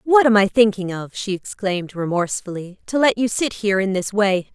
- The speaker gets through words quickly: Yes, fast, 210 wpm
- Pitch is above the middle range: Yes, high, 205 Hz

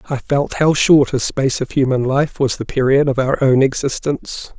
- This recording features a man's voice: Yes, male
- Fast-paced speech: Yes, fast, 210 wpm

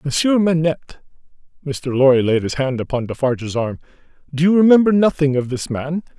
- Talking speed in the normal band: Yes, average, 165 wpm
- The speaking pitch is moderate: Yes, medium, 145 Hz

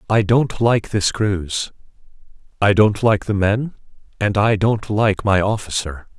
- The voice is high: No, low, 105 Hz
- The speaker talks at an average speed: Yes, average, 155 wpm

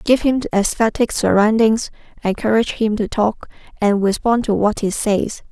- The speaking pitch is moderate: No, high, 215 Hz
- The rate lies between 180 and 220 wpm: No, average, 150 wpm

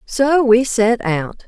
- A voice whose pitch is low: No, high, 235 Hz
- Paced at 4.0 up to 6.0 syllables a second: No, 2.9 syllables/s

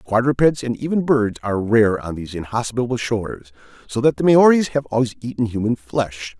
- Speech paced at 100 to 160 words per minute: No, average, 180 wpm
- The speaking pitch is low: Yes, low, 115 Hz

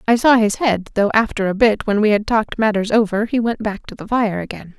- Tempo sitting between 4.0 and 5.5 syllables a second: No, 5.7 syllables/s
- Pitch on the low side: No, high, 215 Hz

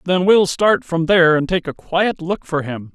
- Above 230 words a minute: Yes, fast, 245 wpm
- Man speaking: Yes, male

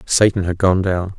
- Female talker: No, male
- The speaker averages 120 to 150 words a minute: No, fast, 205 wpm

